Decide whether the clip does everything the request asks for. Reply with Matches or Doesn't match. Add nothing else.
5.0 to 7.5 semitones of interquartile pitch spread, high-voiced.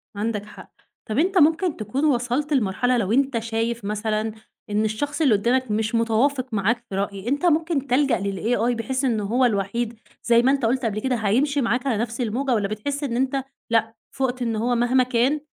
Doesn't match